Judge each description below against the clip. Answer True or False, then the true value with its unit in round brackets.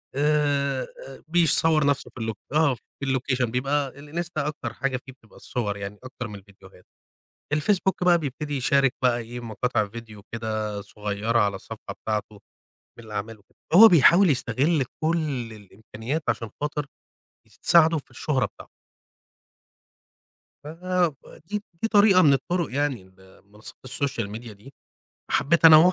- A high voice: False (135 Hz)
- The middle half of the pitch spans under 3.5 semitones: False (5.6 semitones)